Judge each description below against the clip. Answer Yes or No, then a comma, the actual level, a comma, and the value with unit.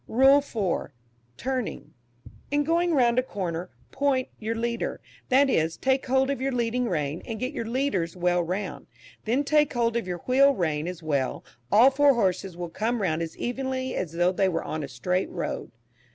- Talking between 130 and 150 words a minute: No, average, 185 wpm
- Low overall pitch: No, high, 230 Hz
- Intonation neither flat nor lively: No, wide, 7.1 semitones